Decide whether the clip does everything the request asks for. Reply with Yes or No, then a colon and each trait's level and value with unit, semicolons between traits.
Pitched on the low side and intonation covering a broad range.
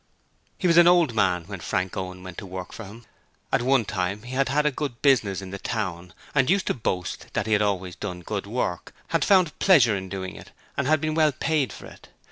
Yes: low, 110 Hz; wide, 7.2 semitones